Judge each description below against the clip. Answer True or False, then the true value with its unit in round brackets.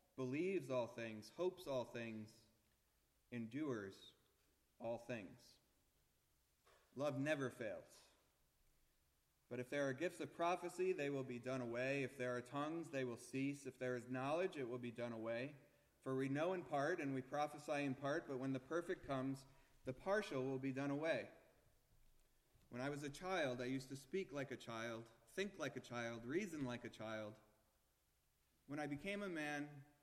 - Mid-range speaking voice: False (130 Hz)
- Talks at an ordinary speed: True (170 wpm)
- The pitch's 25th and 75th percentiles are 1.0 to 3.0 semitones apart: False (3.8 semitones)